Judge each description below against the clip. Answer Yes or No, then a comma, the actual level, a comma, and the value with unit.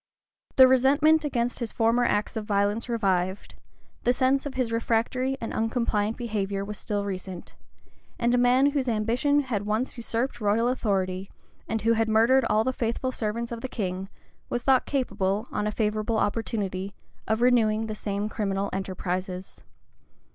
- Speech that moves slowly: No, average, 160 wpm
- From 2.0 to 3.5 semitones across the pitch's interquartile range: Yes, average, 3.2 semitones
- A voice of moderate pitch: No, high, 225 Hz